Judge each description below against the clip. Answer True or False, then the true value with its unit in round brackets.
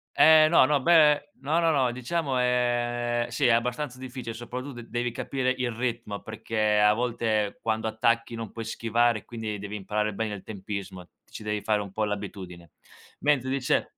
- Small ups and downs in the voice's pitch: False (3.1 semitones)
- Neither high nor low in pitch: False (115 Hz)